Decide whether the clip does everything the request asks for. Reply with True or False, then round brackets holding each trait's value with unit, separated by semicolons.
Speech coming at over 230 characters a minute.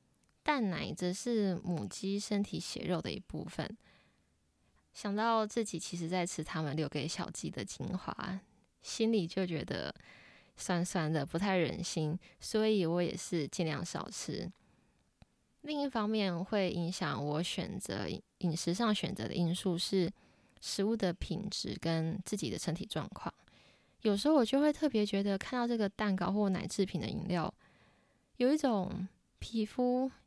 False (220 characters per minute)